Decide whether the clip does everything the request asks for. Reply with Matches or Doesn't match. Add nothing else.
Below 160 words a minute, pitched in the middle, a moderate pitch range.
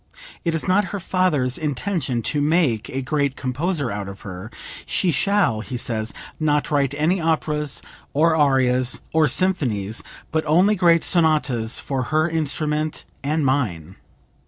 Matches